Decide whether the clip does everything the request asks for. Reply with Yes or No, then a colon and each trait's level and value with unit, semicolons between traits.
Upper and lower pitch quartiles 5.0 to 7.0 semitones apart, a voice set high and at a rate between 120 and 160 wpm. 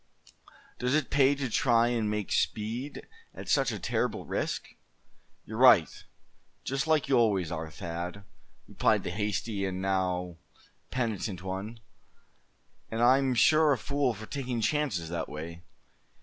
No: wide, 5.5 semitones; low, 110 Hz; average, 140 wpm